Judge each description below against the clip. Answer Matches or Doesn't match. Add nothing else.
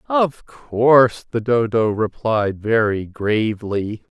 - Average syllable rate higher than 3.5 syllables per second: Doesn't match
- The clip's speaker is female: Doesn't match